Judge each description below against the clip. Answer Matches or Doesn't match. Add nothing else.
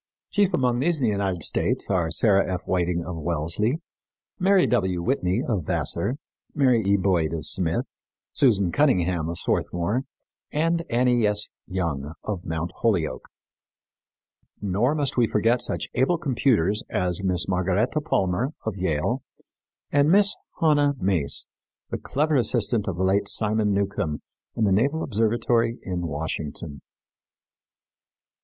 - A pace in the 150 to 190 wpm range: Doesn't match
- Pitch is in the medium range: Doesn't match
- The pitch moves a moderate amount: Doesn't match